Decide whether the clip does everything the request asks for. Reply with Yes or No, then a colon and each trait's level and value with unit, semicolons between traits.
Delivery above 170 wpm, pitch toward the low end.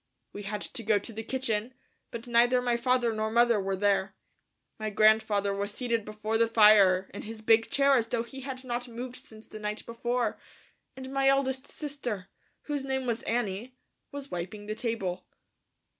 No: average, 180 wpm; high, 230 Hz